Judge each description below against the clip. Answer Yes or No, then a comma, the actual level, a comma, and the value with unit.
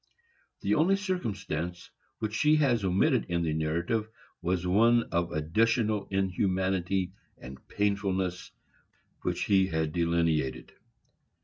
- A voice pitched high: No, very low, 95 Hz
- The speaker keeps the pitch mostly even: No, average, 4.3 semitones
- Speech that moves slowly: Yes, slow, 110 wpm